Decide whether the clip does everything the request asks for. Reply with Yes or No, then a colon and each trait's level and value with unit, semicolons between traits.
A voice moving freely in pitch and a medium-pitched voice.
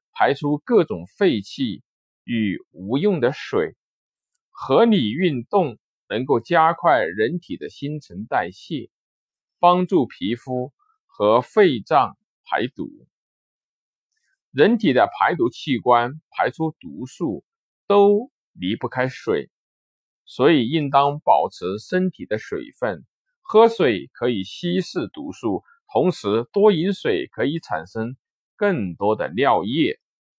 Yes: wide, 8.8 semitones; medium, 160 Hz